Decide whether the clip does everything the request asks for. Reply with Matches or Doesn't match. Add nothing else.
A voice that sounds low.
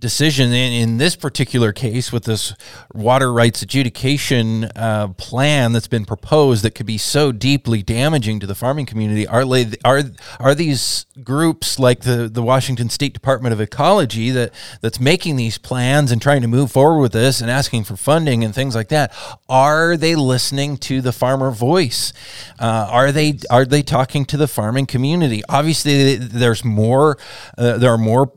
Matches